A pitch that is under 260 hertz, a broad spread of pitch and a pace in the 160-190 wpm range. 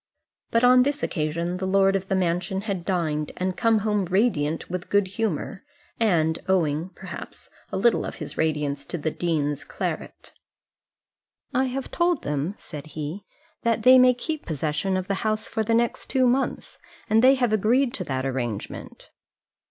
Yes: high, 190 Hz; wide, 6.4 semitones; average, 170 wpm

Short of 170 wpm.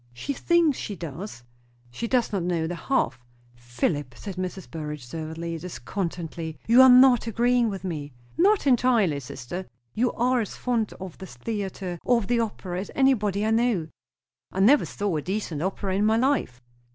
No: average, 175 wpm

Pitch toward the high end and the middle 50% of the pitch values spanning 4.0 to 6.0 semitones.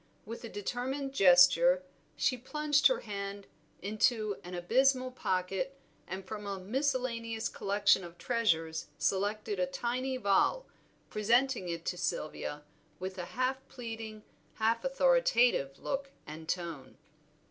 Yes: high, 220 Hz; wide, 5.6 semitones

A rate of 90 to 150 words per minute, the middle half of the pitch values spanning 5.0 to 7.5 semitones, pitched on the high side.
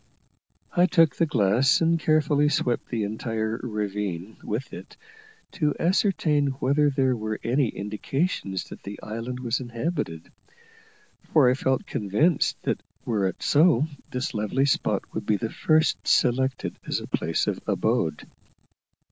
No: average, 140 wpm; wide, 5.6 semitones; low, 125 Hz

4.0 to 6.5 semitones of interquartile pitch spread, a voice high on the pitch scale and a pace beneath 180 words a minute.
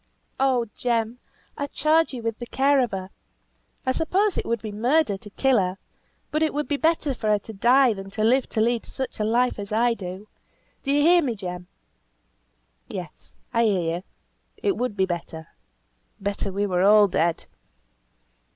No: average, 5.1 semitones; high, 230 Hz; average, 185 wpm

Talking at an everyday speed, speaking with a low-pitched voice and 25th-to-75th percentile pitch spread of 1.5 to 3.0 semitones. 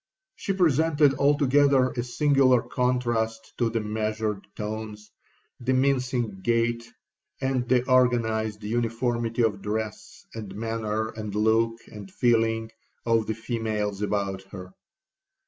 No: slow, 115 wpm; low, 115 Hz; average, 2.7 semitones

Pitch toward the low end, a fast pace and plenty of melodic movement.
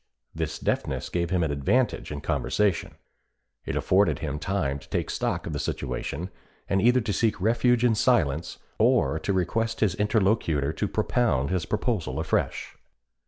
No: very low, 95 Hz; average, 160 wpm; wide, 6.0 semitones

